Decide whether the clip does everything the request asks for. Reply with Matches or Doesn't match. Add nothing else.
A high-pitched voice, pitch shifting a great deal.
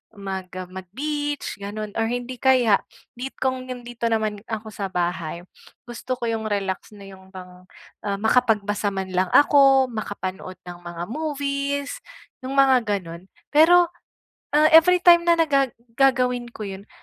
Matches